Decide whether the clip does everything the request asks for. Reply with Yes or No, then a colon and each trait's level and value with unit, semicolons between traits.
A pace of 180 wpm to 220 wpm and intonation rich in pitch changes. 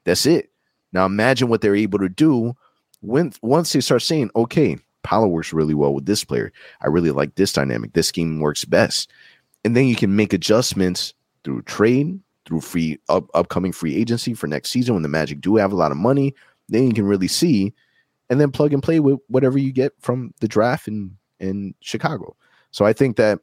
Yes: fast, 205 wpm; wide, 6.2 semitones